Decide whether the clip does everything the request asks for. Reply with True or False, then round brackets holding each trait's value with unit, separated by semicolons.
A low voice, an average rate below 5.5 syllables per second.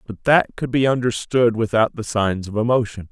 True (115 Hz; 5.1 syllables/s)